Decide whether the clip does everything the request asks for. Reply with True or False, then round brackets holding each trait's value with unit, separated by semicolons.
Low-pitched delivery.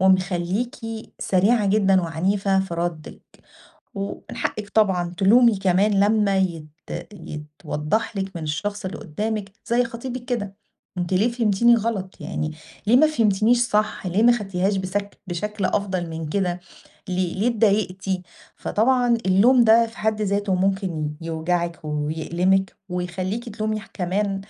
False (195 Hz)